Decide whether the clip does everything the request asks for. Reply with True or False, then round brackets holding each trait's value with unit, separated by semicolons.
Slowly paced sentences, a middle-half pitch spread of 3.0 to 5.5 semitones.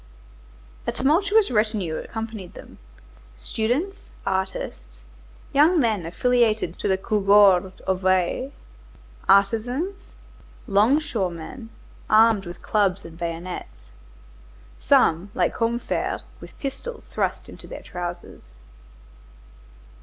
True (90 wpm; 5.2 semitones)